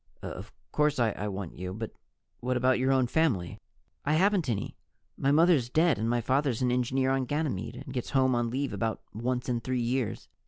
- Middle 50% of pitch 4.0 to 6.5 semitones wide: No, average, 2.8 semitones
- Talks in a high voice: No, low, 125 Hz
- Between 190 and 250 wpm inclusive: Yes, average, 195 wpm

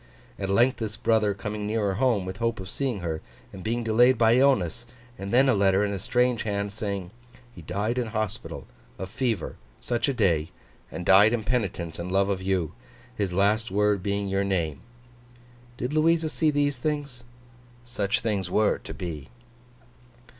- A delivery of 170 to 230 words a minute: Yes, average, 175 wpm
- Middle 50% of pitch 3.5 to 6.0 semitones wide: Yes, average, 3.8 semitones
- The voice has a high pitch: No, low, 105 Hz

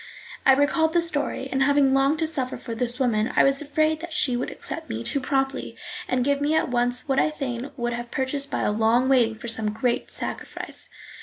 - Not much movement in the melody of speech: No, average, 3.0 semitones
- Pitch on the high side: Yes, very high, 265 Hz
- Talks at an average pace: No, fast, 215 wpm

